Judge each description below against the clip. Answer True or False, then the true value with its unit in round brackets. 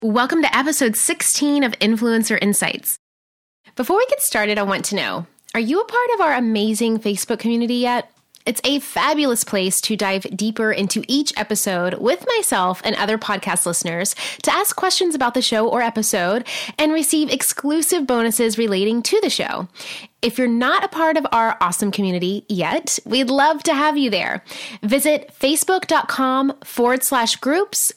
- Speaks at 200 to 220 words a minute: False (165 wpm)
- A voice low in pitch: False (235 Hz)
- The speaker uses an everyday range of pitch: False (5.7 semitones)